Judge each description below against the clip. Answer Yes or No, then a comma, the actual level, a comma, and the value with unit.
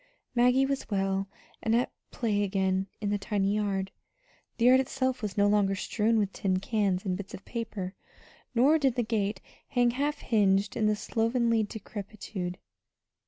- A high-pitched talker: Yes, high, 210 Hz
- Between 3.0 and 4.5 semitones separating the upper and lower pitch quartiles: Yes, average, 3.4 semitones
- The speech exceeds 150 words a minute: Yes, average, 160 wpm